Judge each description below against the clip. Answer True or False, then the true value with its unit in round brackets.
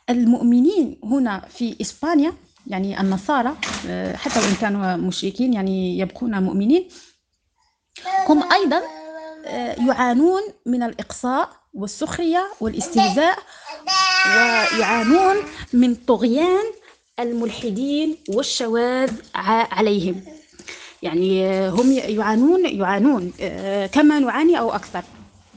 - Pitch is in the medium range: False (250 Hz)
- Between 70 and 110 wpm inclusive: True (80 wpm)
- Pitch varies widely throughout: True (7.1 semitones)